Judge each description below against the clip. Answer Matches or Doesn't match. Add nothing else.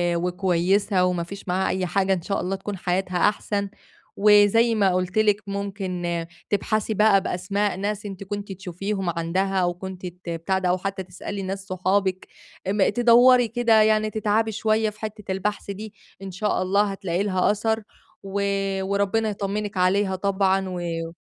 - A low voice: Doesn't match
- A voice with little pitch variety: Matches